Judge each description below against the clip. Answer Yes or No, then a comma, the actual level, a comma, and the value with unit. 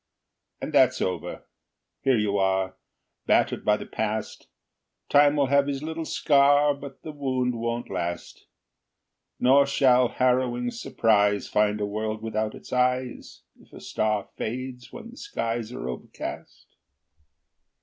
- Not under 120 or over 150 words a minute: Yes, slow, 135 wpm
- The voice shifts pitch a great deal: No, average, 4.5 semitones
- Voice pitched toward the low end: Yes, low, 125 Hz